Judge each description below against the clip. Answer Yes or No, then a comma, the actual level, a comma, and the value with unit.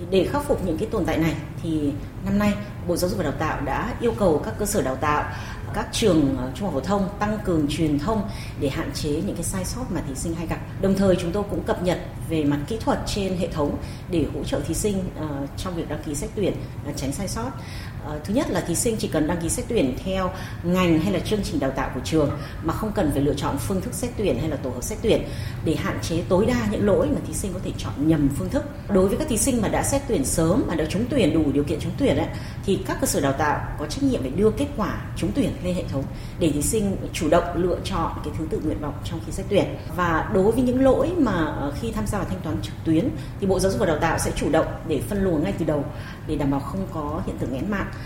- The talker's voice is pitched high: No, medium, 145 Hz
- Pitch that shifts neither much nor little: Yes, average, 3.8 semitones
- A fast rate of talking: Yes, fast, 275 wpm